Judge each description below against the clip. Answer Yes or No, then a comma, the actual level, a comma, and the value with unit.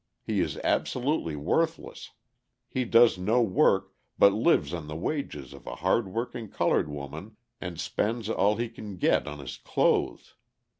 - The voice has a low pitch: Yes, low, 100 Hz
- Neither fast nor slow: Yes, average, 155 wpm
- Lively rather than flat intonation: Yes, wide, 7.0 semitones